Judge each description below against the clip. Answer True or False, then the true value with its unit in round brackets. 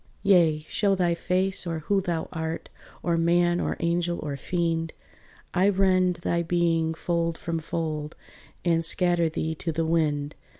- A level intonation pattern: True (1.6 semitones)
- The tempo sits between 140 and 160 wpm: True (155 wpm)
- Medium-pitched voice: True (170 Hz)